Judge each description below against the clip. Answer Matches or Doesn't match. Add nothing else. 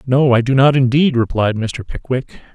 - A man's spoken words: Matches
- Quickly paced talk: Doesn't match